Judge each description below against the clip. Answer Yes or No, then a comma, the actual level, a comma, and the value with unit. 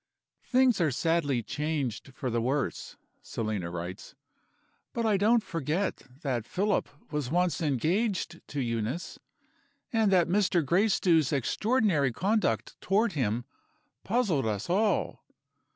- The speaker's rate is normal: No, slow, 120 wpm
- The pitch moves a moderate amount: No, wide, 7.8 semitones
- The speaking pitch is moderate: Yes, medium, 165 Hz